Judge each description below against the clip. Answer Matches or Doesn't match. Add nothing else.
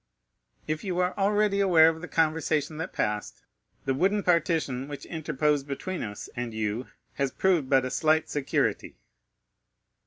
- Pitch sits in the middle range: Matches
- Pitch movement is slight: Doesn't match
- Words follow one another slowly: Doesn't match